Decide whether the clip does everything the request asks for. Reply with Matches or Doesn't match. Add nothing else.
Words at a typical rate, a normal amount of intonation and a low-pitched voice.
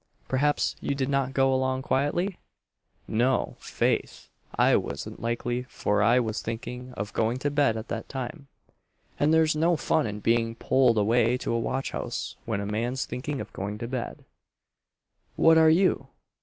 Matches